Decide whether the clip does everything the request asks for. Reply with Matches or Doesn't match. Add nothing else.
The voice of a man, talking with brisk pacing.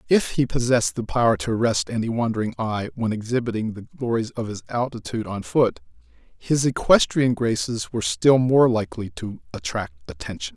Doesn't match